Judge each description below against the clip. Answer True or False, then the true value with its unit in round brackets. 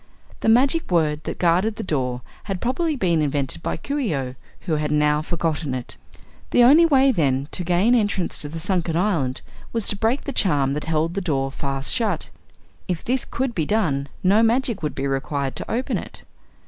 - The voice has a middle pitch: True (170 Hz)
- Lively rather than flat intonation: True (7.3 semitones)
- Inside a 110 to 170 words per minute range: False (200 wpm)